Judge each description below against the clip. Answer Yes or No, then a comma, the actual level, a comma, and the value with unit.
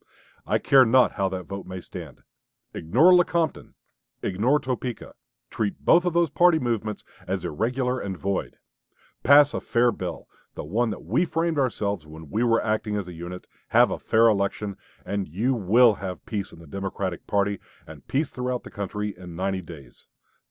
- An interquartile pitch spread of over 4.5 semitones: Yes, average, 5.1 semitones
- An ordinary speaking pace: Yes, average, 175 wpm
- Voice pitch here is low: Yes, low, 105 Hz